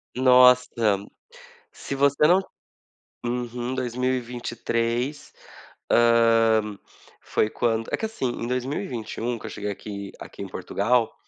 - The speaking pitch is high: No, low, 120 Hz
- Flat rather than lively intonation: Yes, narrow, 1.9 semitones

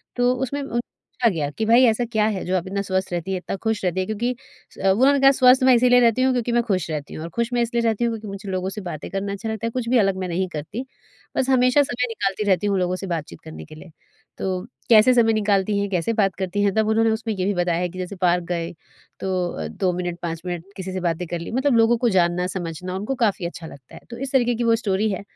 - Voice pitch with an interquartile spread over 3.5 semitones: Yes, average, 4.6 semitones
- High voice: Yes, high, 200 Hz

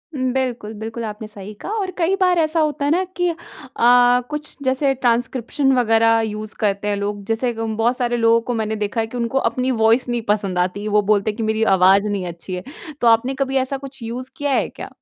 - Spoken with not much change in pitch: No, average, 3.9 semitones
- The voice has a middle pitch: No, high, 230 Hz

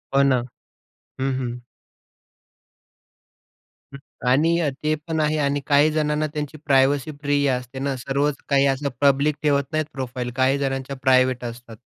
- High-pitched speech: No, medium, 140 Hz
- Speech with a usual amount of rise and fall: No, narrow, 2.2 semitones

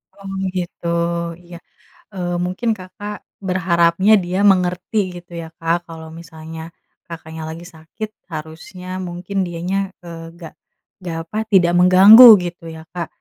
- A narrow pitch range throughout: Yes, narrow, 2.0 semitones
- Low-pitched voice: No, medium, 175 Hz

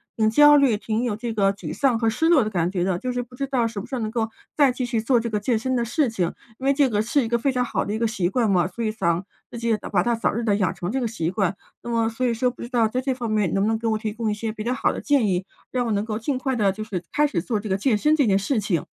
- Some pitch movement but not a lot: Yes, average, 3.2 semitones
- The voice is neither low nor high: No, high, 225 Hz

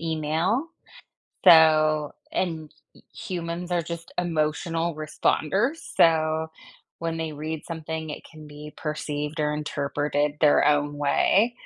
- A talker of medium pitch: Yes, medium, 155 Hz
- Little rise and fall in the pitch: Yes, narrow, 1.8 semitones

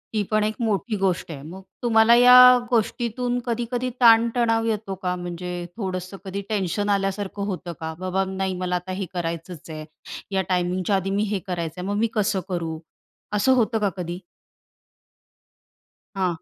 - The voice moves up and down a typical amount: Yes, average, 3.7 semitones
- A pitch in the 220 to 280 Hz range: No, high, 195 Hz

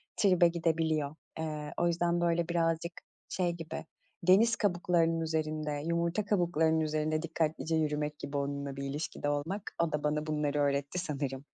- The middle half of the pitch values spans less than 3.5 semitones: Yes, narrow, 2.4 semitones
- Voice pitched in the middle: Yes, medium, 160 Hz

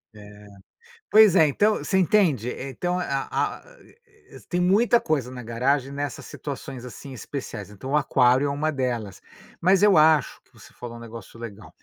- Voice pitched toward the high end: No, medium, 140 Hz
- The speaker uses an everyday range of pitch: No, wide, 6.8 semitones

